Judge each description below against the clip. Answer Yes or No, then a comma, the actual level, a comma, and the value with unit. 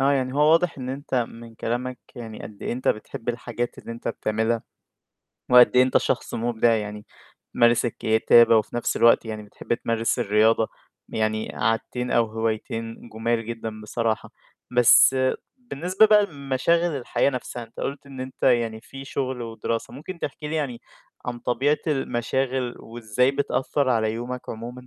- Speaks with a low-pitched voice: Yes, low, 120 Hz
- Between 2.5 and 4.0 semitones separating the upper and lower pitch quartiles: Yes, average, 2.8 semitones